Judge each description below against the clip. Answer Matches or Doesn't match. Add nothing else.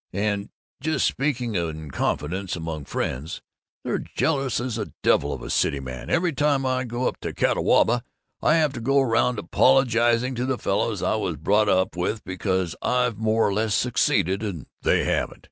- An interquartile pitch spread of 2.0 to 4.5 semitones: Doesn't match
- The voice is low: Matches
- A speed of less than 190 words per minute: Matches